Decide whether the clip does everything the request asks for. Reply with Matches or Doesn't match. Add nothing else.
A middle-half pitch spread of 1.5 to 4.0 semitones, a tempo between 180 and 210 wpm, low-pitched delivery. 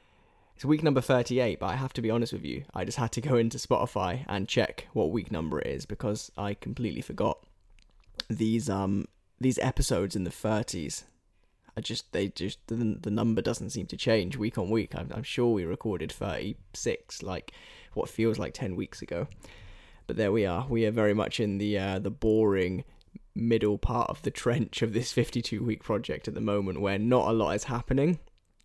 Matches